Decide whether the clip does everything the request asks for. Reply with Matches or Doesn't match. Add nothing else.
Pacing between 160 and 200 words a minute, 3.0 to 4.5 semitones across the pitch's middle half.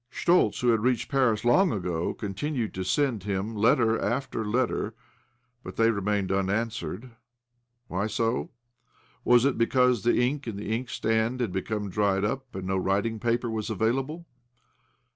Doesn't match